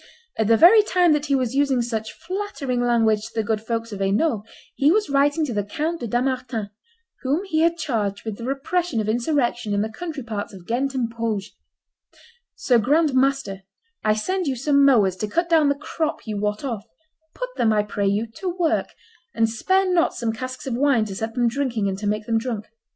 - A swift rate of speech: Yes, fast, 210 wpm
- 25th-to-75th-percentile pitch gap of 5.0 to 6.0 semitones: Yes, wide, 5.4 semitones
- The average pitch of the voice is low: No, high, 245 Hz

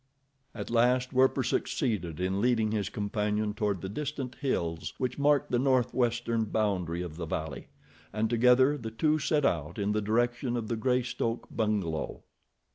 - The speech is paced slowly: No, average, 155 wpm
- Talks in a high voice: No, low, 115 Hz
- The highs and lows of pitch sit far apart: No, average, 3.7 semitones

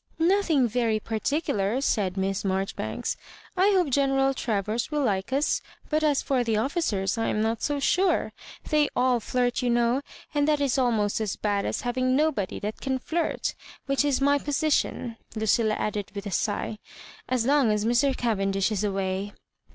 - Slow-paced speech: No, average, 180 wpm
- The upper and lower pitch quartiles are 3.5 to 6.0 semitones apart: Yes, average, 5.1 semitones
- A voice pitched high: Yes, high, 240 Hz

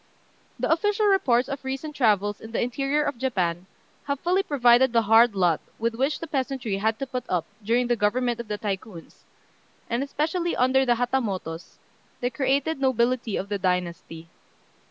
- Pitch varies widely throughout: No, average, 4.7 semitones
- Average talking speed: Yes, average, 175 wpm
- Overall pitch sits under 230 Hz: No, high, 240 Hz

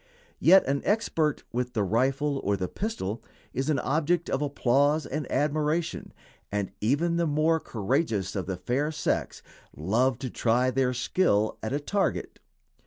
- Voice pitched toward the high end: No, low, 135 Hz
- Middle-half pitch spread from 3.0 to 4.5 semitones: No, average, 5.2 semitones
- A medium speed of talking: Yes, average, 155 wpm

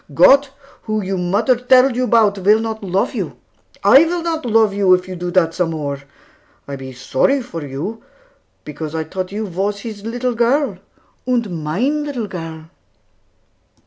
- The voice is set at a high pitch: Yes, high, 205 Hz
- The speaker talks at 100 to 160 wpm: No, average, 170 wpm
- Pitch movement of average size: No, wide, 5.9 semitones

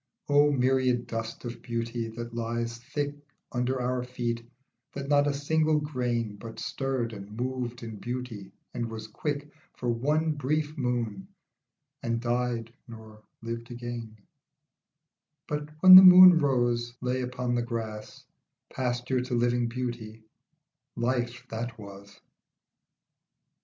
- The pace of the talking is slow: Yes, slow, 125 wpm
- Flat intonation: Yes, narrow, 2.1 semitones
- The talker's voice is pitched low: Yes, low, 120 Hz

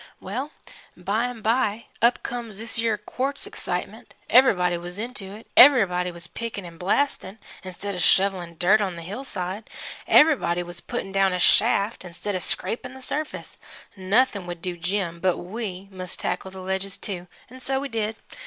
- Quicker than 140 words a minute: Yes, average, 170 wpm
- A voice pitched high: Yes, high, 195 Hz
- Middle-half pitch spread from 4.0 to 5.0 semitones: Yes, average, 4.4 semitones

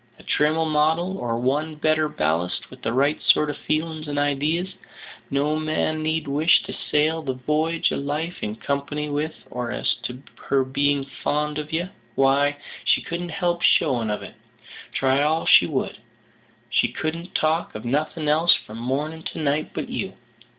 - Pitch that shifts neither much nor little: No, narrow, 2.3 semitones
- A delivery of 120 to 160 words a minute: No, average, 170 wpm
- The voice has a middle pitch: Yes, medium, 150 Hz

